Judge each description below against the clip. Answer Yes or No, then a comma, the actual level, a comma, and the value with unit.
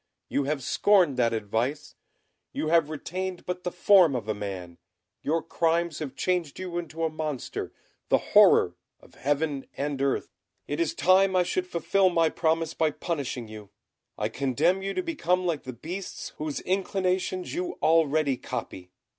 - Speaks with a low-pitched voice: No, medium, 160 Hz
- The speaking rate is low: No, average, 165 wpm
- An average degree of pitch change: Yes, average, 4.8 semitones